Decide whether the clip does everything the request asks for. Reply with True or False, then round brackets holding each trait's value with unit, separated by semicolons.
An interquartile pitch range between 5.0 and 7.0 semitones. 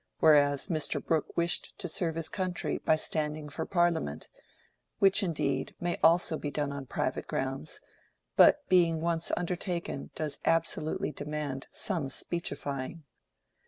False (3.0 semitones)